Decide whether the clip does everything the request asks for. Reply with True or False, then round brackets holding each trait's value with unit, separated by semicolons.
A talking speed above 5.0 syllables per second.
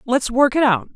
False (4.9 syllables/s)